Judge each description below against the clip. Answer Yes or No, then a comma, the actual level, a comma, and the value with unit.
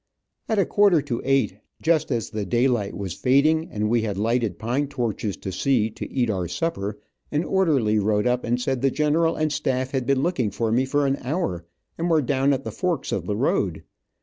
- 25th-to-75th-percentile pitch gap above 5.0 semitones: Yes, wide, 5.4 semitones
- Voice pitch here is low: Yes, low, 125 Hz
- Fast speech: Yes, fast, 210 wpm